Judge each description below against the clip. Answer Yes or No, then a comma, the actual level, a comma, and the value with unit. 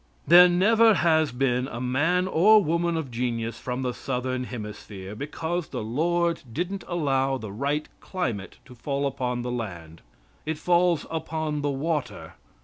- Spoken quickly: No, average, 150 wpm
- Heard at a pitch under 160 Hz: Yes, medium, 140 Hz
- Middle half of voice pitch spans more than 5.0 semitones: Yes, wide, 5.5 semitones